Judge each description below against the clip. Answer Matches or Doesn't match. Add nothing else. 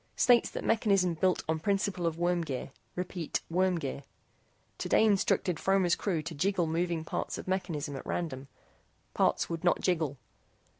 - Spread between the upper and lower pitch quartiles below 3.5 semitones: Matches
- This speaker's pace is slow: Doesn't match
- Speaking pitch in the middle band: Matches